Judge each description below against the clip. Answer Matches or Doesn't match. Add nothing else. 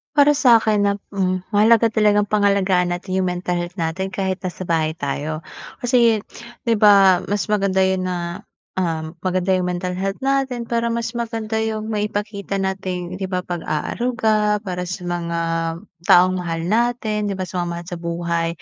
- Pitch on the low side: Doesn't match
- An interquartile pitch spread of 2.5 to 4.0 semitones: Matches